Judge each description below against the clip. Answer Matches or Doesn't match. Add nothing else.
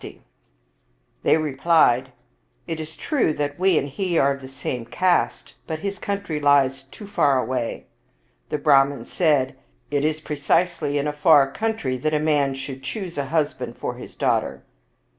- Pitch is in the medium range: Matches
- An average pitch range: Matches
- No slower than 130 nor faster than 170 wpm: Doesn't match